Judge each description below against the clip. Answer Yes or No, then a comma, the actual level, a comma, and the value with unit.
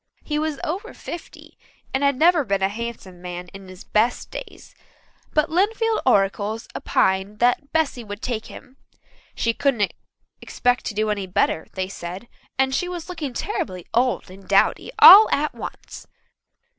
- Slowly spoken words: No, average, 155 wpm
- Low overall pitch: No, high, 240 Hz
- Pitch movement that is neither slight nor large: No, wide, 7.6 semitones